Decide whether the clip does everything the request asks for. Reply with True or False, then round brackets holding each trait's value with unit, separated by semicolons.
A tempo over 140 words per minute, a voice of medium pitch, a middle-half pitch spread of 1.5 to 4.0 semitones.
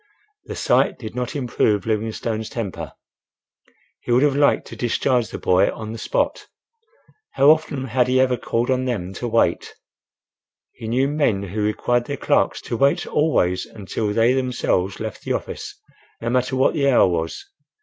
False (170 wpm; 120 Hz; 3.3 semitones)